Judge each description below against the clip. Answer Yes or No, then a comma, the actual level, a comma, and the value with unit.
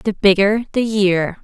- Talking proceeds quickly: No, average, 165 wpm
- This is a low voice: No, high, 200 Hz